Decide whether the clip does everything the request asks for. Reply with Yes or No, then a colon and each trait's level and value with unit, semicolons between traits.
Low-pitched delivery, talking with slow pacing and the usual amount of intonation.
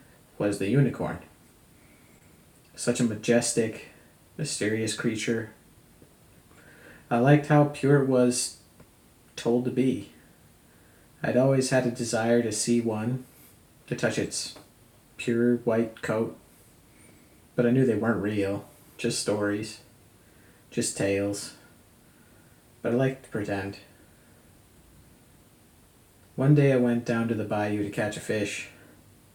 Yes: low, 115 Hz; slow, 120 wpm; average, 3.1 semitones